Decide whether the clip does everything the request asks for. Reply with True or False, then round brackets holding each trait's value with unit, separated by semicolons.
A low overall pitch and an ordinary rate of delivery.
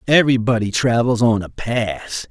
False (115 Hz; 130 wpm)